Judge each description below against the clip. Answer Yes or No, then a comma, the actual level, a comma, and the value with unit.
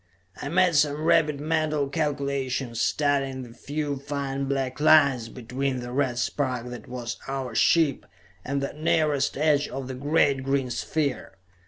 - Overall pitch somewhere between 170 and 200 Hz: No, medium, 140 Hz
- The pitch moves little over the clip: Yes, narrow, 2.3 semitones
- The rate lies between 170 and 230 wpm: No, average, 150 wpm